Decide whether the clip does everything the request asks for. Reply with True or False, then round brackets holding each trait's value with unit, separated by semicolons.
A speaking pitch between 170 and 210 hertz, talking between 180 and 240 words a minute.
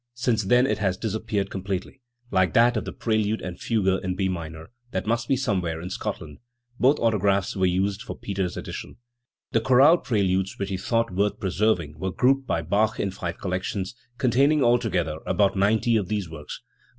False (100 Hz; 185 wpm)